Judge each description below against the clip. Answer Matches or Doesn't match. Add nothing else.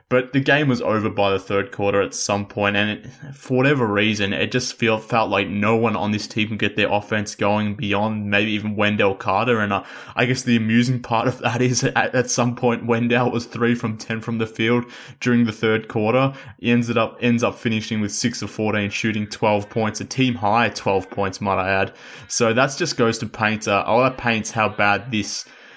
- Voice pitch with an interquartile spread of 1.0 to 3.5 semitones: Matches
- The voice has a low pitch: Matches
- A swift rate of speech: Matches